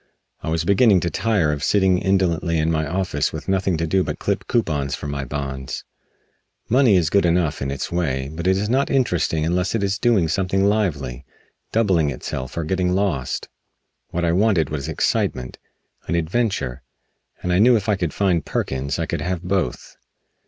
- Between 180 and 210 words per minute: Yes, average, 190 wpm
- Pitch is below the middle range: Yes, very low, 85 Hz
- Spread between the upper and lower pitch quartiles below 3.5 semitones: No, average, 4.5 semitones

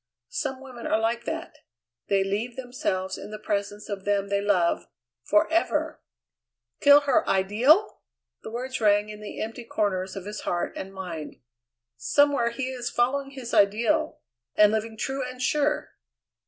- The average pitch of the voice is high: Yes, high, 225 Hz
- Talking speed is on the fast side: No, average, 155 wpm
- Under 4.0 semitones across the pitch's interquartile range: No, average, 4.6 semitones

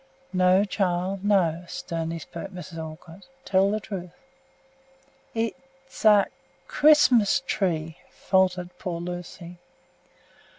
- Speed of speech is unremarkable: No, slow, 95 wpm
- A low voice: No, medium, 185 Hz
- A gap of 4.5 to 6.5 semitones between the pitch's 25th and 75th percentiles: No, average, 3.0 semitones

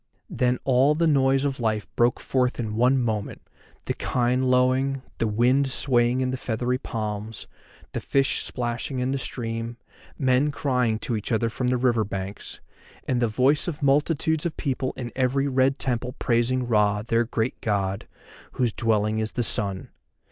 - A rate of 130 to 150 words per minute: No, average, 165 wpm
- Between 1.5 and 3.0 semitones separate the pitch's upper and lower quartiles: Yes, average, 2.7 semitones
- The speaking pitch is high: No, low, 125 Hz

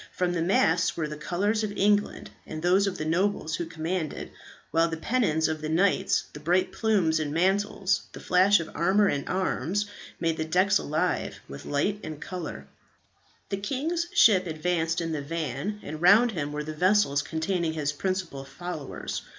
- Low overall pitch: No, medium, 170 Hz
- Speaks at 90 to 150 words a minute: No, average, 175 wpm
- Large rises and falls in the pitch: No, average, 4.0 semitones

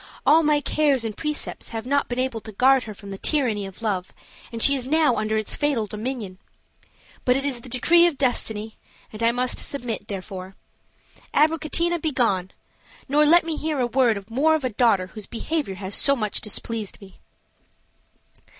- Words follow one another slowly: No, average, 180 wpm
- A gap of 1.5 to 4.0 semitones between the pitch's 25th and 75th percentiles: No, wide, 5.4 semitones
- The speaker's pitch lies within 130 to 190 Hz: No, high, 245 Hz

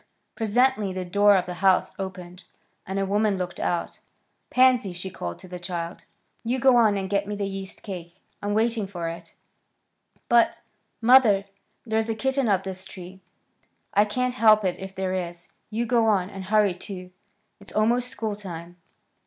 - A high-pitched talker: Yes, high, 195 Hz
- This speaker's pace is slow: No, average, 175 wpm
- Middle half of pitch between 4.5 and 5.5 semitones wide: No, average, 3.1 semitones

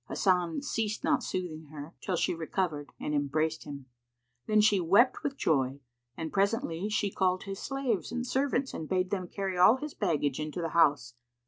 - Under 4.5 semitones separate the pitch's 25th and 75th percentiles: No, average, 5.3 semitones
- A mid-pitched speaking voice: Yes, medium, 180 Hz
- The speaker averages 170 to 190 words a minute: Yes, average, 180 wpm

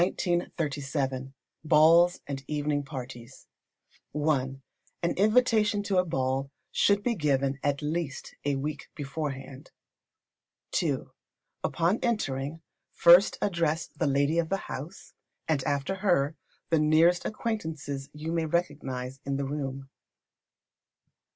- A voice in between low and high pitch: Yes, medium, 150 Hz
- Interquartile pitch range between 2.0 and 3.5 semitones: No, average, 3.9 semitones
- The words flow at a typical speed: No, slow, 110 wpm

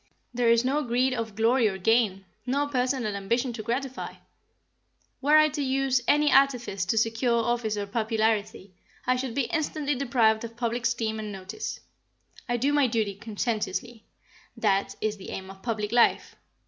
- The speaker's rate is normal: Yes, average, 165 wpm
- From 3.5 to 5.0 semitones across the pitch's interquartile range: No, average, 3.1 semitones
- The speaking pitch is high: Yes, high, 235 Hz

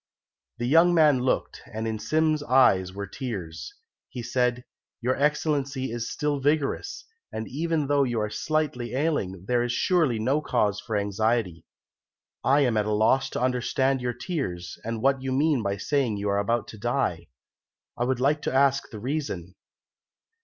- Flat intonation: No, average, 4.6 semitones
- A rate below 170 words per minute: No, average, 175 wpm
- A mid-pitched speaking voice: No, low, 125 Hz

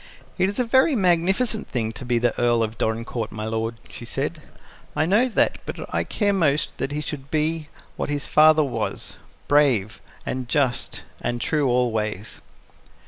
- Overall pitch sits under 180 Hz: Yes, medium, 140 Hz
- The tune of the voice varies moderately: No, wide, 6.0 semitones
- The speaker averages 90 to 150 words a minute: No, average, 170 wpm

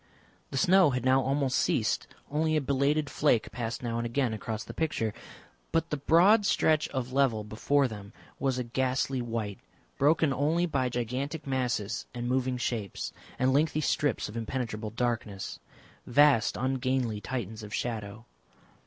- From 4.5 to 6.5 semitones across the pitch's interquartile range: No, average, 3.7 semitones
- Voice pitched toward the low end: Yes, low, 130 Hz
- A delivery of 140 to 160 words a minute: Yes, average, 155 wpm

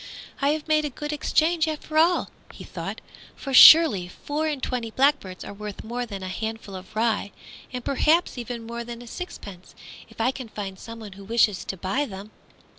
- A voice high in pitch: Yes, high, 235 Hz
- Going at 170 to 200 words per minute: Yes, average, 190 wpm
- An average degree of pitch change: No, wide, 6.3 semitones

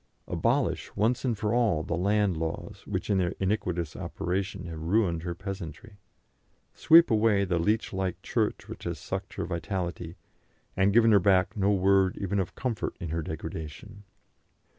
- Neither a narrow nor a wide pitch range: Yes, average, 3.4 semitones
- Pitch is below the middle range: Yes, very low, 95 Hz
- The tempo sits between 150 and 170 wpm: Yes, average, 165 wpm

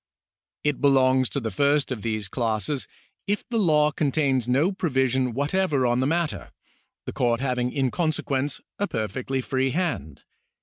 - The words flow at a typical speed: Yes, average, 160 wpm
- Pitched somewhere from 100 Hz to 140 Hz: Yes, low, 135 Hz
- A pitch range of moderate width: Yes, average, 3.3 semitones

